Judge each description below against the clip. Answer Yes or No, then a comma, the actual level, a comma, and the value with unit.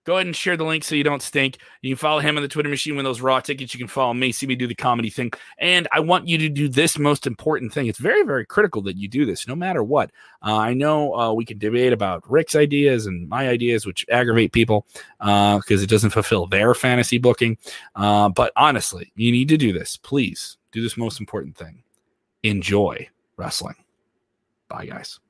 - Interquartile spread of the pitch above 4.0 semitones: Yes, average, 4.9 semitones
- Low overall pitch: Yes, low, 125 Hz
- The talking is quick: Yes, fast, 225 wpm